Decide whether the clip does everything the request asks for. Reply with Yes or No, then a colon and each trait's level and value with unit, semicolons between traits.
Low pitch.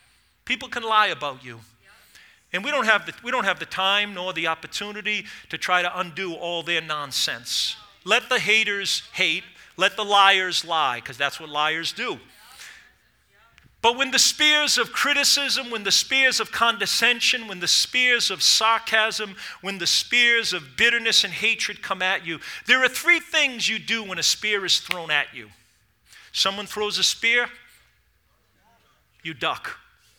No: high, 210 Hz